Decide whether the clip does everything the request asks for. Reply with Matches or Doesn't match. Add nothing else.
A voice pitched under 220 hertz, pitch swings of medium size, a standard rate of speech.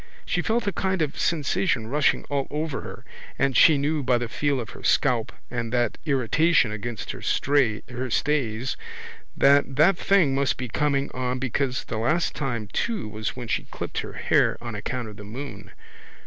Matches